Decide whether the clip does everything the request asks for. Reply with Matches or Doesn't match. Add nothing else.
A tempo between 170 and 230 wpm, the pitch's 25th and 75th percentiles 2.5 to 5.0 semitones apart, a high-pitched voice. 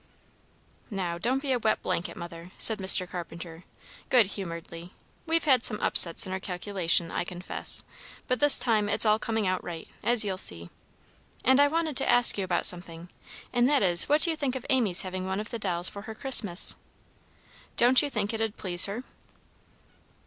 Doesn't match